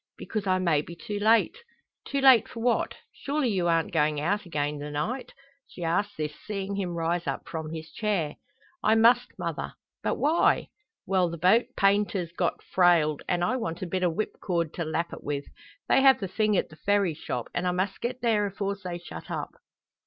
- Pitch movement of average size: Yes, average, 4.3 semitones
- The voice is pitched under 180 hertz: No, medium, 185 Hz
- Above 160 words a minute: Yes, average, 200 wpm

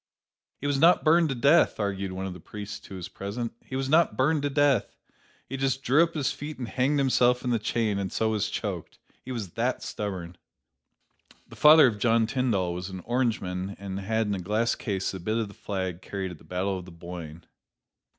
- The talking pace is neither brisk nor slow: No, fast, 220 wpm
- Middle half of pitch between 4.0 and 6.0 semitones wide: Yes, wide, 5.6 semitones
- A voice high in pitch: No, low, 110 Hz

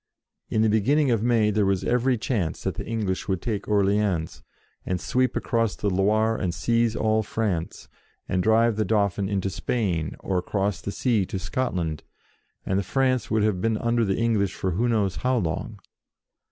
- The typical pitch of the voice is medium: No, low, 105 Hz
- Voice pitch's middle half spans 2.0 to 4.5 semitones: Yes, average, 3.2 semitones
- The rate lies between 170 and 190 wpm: Yes, average, 180 wpm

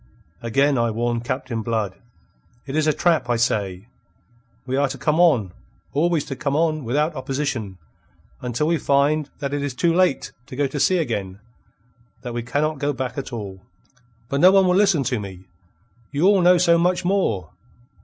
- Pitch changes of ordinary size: Yes, average, 4.8 semitones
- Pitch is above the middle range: No, medium, 140 Hz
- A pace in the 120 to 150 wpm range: No, average, 185 wpm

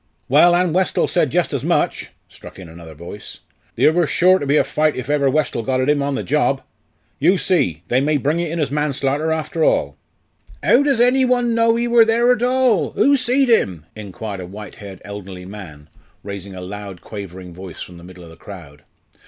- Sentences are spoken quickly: Yes, fast, 210 wpm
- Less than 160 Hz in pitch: Yes, medium, 140 Hz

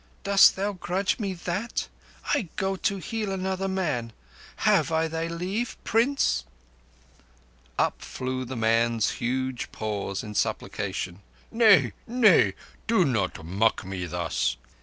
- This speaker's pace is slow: Yes, slow, 115 wpm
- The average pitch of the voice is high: No, medium, 165 Hz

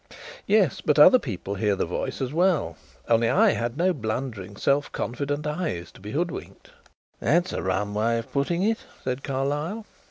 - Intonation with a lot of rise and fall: Yes, wide, 7.8 semitones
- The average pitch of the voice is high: No, low, 135 Hz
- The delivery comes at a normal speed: Yes, average, 170 wpm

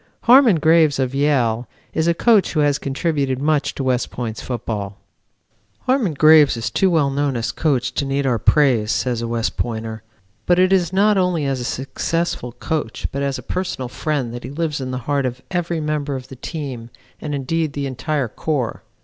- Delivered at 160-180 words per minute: No, average, 200 wpm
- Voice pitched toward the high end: No, medium, 140 Hz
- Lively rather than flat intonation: No, average, 4.1 semitones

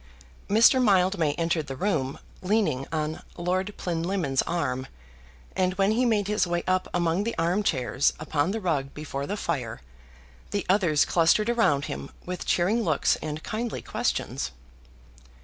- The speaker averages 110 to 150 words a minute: Yes, average, 145 wpm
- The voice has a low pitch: No, medium, 175 Hz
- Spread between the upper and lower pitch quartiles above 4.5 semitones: Yes, average, 5.2 semitones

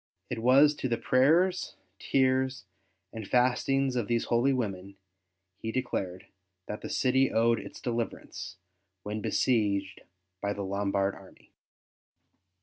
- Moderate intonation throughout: Yes, average, 4.4 semitones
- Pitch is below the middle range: Yes, low, 115 Hz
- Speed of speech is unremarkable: No, slow, 125 wpm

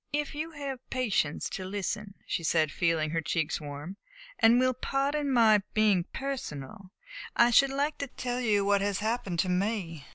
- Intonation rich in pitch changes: Yes, wide, 6.5 semitones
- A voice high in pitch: Yes, high, 210 Hz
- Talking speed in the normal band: Yes, average, 170 wpm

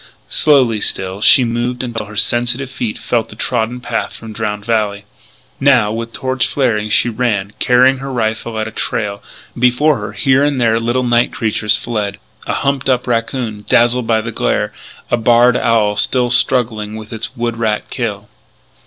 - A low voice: Yes, low, 115 Hz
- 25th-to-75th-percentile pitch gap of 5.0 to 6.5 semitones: No, narrow, 2.5 semitones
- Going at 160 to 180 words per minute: Yes, average, 170 wpm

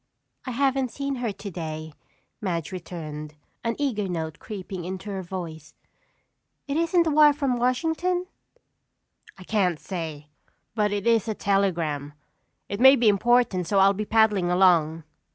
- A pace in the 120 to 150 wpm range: Yes, average, 145 wpm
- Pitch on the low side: No, high, 200 Hz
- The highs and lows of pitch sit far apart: Yes, wide, 6.2 semitones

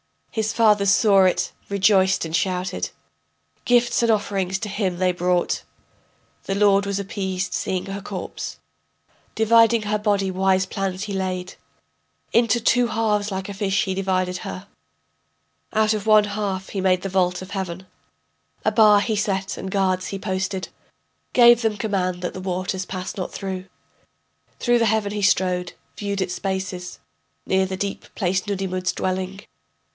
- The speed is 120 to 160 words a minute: Yes, average, 155 wpm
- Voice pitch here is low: No, high, 195 Hz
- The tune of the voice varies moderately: No, narrow, 1.9 semitones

